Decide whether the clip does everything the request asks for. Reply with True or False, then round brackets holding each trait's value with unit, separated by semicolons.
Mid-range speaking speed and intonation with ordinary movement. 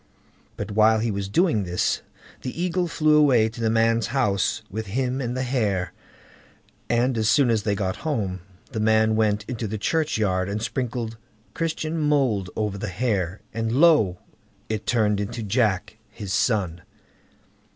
True (160 wpm; 3.7 semitones)